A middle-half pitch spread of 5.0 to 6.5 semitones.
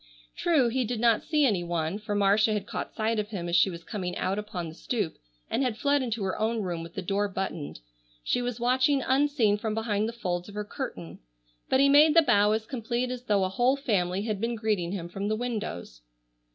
No: average, 4.3 semitones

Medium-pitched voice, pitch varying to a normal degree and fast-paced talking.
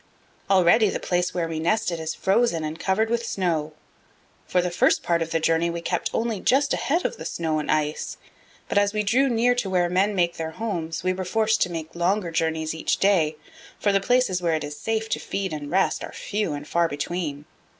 Yes: medium, 175 Hz; average, 4.3 semitones; fast, 220 wpm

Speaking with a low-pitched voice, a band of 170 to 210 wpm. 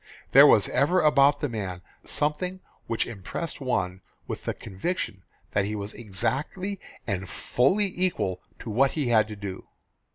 No: low, 120 Hz; average, 155 wpm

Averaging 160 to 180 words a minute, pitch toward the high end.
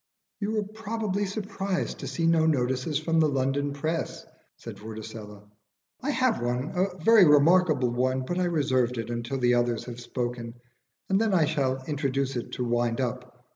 No: average, 175 wpm; medium, 140 Hz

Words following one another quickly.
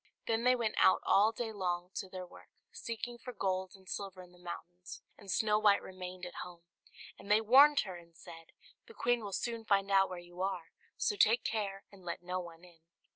Yes: fast, 215 wpm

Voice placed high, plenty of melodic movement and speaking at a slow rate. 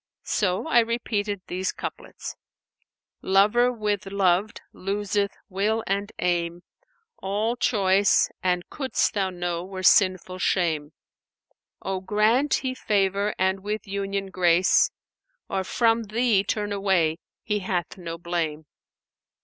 No: high, 195 Hz; narrow, 2.6 semitones; slow, 125 wpm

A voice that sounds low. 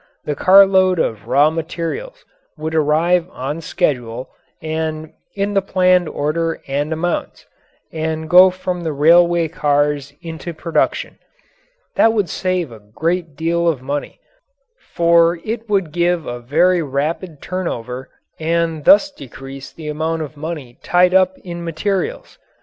No: medium, 165 Hz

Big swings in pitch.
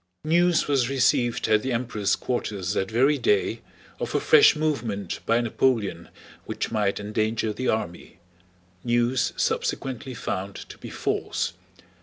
No: average, 4.6 semitones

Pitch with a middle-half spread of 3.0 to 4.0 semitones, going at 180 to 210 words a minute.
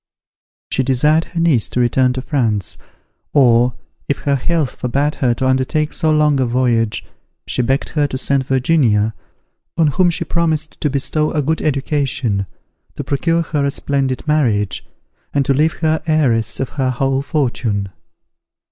No: average, 3.6 semitones; average, 165 wpm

